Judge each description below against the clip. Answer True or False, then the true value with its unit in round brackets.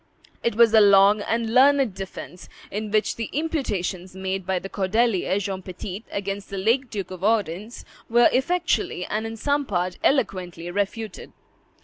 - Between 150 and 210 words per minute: True (155 wpm)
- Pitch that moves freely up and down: False (3.4 semitones)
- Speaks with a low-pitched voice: False (205 Hz)